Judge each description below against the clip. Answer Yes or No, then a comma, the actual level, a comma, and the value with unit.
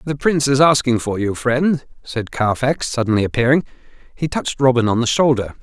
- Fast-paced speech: No, average, 180 wpm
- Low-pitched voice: Yes, low, 130 Hz